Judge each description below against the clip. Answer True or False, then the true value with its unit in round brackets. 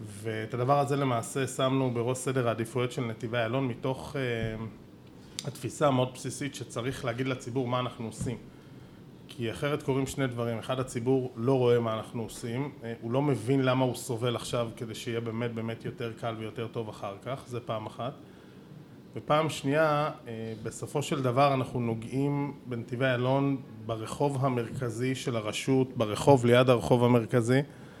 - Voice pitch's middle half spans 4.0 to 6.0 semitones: False (2.8 semitones)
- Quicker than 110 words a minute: True (150 wpm)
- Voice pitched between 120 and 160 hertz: True (125 Hz)